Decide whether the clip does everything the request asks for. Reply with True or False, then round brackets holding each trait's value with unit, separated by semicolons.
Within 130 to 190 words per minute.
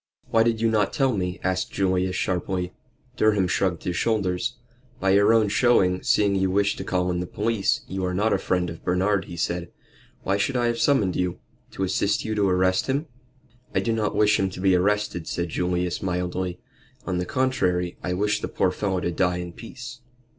False (205 wpm)